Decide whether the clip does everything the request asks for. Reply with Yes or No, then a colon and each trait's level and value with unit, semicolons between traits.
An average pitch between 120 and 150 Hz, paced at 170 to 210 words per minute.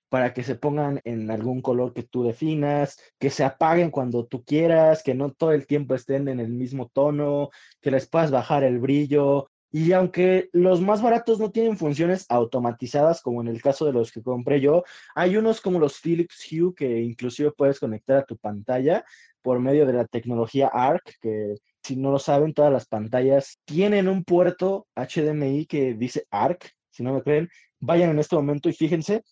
Yes: medium, 140 Hz; fast, 190 wpm